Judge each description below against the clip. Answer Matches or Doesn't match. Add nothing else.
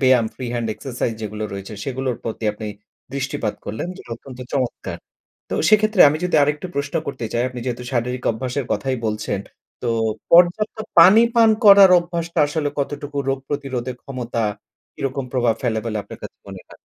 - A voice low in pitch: Matches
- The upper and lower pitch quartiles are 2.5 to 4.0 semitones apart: Matches